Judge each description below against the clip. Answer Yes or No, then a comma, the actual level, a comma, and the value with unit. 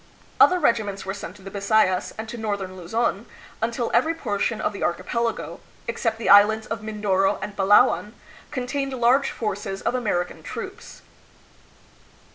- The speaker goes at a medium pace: Yes, average, 150 wpm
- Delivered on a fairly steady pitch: No, average, 3.0 semitones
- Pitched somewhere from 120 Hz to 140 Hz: No, high, 215 Hz